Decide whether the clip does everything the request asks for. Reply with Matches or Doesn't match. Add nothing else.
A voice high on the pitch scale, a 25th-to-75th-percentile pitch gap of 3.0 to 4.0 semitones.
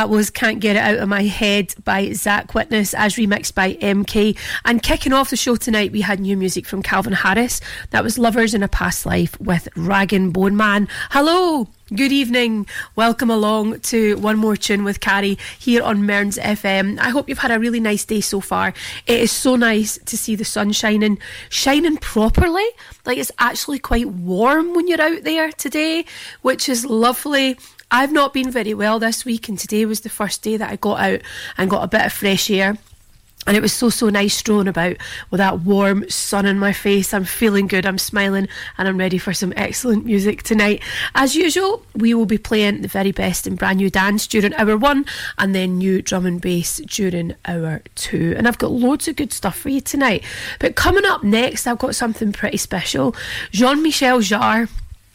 Matches